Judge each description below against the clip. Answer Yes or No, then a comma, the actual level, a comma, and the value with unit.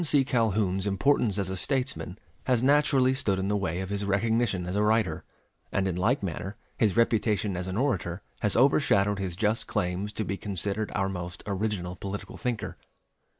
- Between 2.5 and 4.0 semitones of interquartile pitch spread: Yes, average, 3.1 semitones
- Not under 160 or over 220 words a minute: Yes, average, 175 wpm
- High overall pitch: No, low, 100 Hz